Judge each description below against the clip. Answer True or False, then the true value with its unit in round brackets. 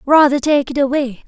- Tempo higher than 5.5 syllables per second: False (5.3 syllables/s)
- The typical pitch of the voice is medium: False (275 Hz)